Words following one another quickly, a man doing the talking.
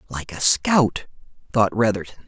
No: slow, 130 wpm; male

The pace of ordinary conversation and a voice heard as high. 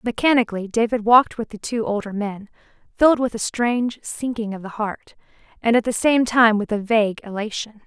Yes: average, 190 wpm; high, 225 Hz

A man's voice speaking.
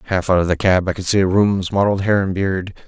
Yes: male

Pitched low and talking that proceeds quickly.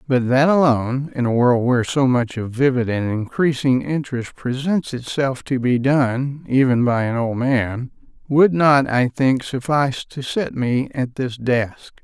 No: low, 130 Hz; average, 175 wpm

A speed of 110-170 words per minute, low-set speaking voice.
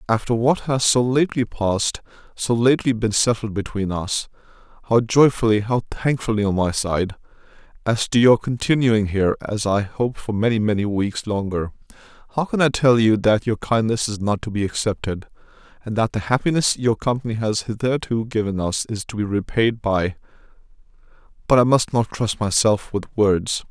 Yes: average, 160 wpm; low, 110 Hz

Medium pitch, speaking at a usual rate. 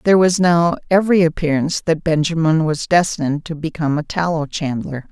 Yes: medium, 160 Hz; average, 165 wpm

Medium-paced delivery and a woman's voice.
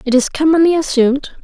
Yes: average, 170 wpm; female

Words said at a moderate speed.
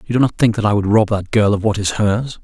No: fast, 345 wpm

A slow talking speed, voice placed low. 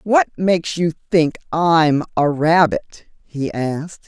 No: slow, 130 wpm; medium, 165 Hz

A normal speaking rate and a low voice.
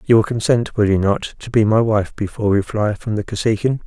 No: fast, 250 wpm; low, 110 Hz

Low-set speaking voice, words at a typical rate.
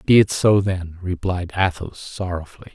Yes: very low, 90 Hz; average, 155 wpm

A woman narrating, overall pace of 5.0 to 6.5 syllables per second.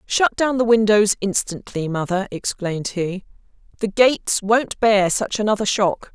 No: female; 4.5 syllables/s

